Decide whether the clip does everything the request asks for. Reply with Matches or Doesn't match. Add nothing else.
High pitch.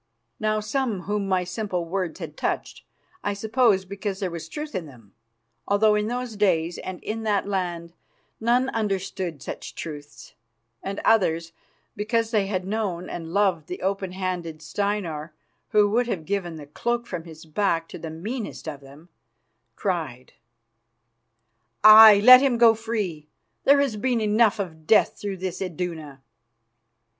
Matches